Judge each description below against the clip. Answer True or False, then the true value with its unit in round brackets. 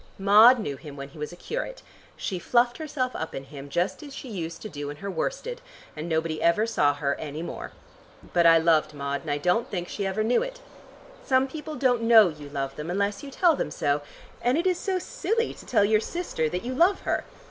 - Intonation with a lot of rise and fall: True (9.0 semitones)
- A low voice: False (195 Hz)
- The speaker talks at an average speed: False (230 wpm)